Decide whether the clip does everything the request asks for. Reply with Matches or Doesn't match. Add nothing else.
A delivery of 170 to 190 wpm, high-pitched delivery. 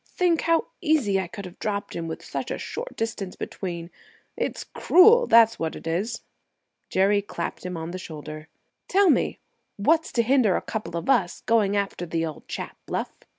Matches